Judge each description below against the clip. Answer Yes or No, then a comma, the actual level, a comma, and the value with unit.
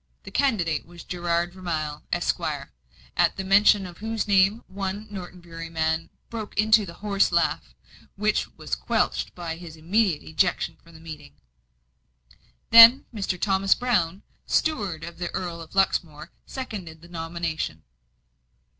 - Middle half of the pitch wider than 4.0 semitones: No, average, 3.7 semitones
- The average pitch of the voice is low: No, medium, 180 Hz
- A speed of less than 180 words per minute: Yes, average, 140 wpm